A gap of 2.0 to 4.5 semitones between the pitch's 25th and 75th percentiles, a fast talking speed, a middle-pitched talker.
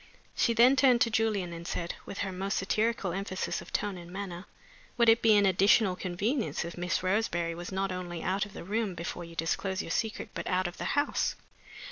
No: average, 3.7 semitones; fast, 210 wpm; high, 195 Hz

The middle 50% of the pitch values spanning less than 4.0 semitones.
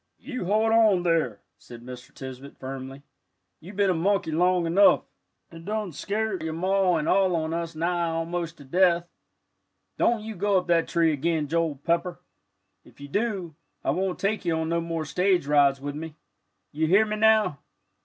Yes: average, 3.6 semitones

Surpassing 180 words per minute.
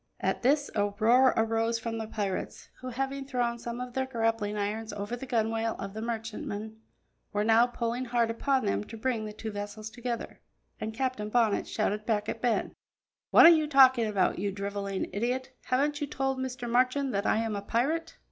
Yes: average, 195 wpm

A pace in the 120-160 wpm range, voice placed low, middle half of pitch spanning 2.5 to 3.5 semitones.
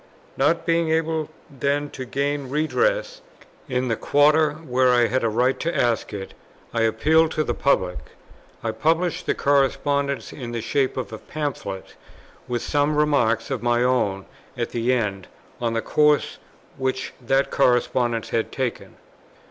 No: average, 155 wpm; low, 130 Hz; average, 4.1 semitones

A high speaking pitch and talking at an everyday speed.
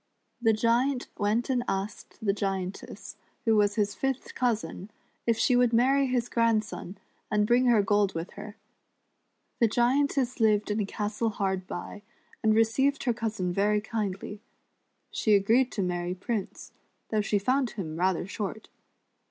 Yes: high, 215 Hz; average, 150 wpm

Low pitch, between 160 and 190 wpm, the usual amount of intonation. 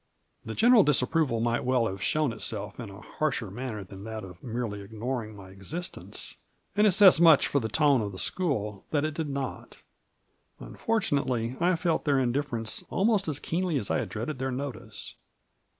No: low, 130 Hz; average, 180 wpm; wide, 6.0 semitones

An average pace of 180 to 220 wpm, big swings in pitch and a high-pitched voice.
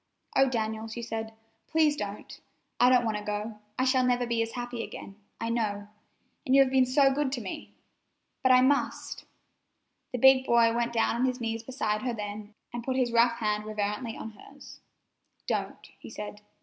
No: average, 190 wpm; average, 2.9 semitones; high, 235 Hz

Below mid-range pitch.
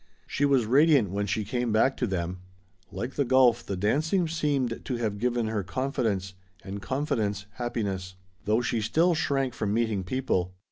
Yes: low, 115 Hz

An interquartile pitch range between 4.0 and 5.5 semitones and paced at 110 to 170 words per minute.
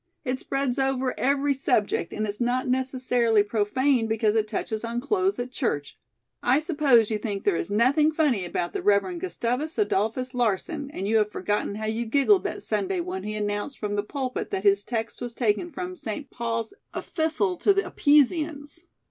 No: average, 5.2 semitones; average, 180 wpm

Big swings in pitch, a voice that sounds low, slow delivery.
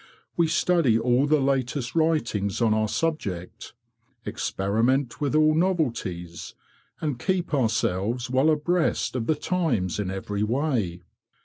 Yes: wide, 6.4 semitones; low, 125 Hz; slow, 125 wpm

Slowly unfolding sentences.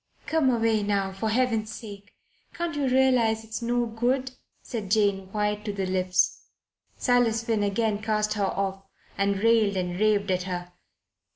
No: average, 160 wpm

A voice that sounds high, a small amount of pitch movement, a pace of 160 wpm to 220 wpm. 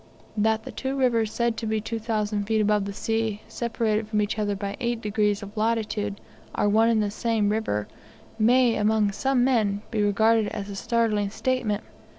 Yes: high, 220 Hz; narrow, 1.7 semitones; average, 180 wpm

